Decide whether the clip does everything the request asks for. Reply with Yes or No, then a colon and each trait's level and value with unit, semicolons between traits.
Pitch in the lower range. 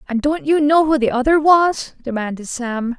No: very high, 270 Hz